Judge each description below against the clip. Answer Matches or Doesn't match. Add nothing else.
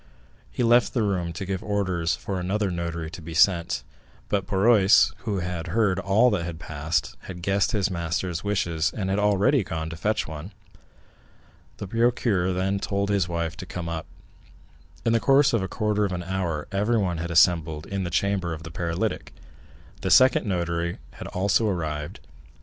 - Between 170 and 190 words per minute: Matches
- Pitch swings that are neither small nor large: Matches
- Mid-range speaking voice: Doesn't match